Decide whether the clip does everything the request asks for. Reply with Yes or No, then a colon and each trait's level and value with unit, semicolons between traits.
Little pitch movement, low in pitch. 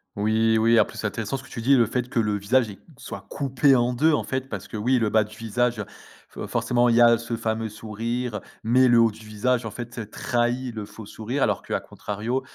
Yes: narrow, 2.2 semitones; low, 115 Hz